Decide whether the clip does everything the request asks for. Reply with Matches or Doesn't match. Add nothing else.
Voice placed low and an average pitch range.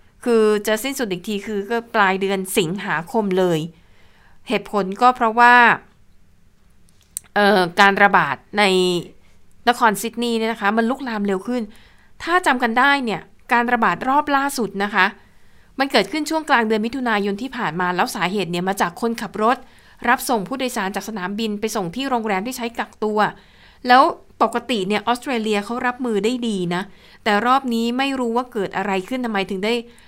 Doesn't match